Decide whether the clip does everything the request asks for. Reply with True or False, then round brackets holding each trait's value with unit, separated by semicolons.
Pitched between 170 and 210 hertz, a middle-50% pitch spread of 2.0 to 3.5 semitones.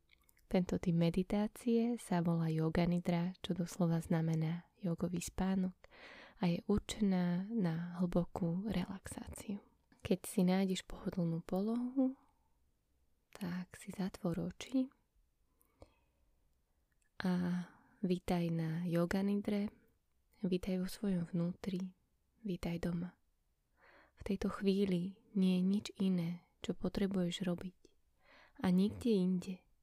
True (185 Hz; 2.4 semitones)